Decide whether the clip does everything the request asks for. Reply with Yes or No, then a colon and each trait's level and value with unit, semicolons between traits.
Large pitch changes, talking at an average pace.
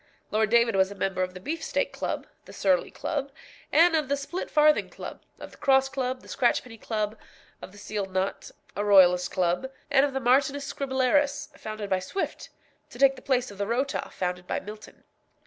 Yes: wide, 5.7 semitones; average, 190 wpm